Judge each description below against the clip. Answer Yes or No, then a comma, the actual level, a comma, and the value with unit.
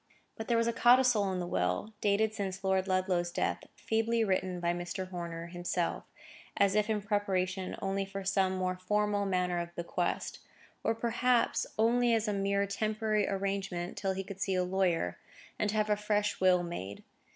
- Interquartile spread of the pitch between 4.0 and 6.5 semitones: No, narrow, 2.6 semitones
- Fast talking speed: No, average, 175 wpm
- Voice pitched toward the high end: Yes, high, 195 Hz